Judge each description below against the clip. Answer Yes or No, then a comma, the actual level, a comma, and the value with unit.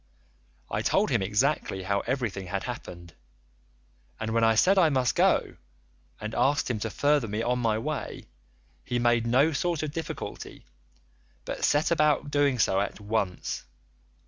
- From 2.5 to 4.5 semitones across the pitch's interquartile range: No, average, 5.3 semitones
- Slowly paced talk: No, average, 155 wpm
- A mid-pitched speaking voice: No, low, 120 Hz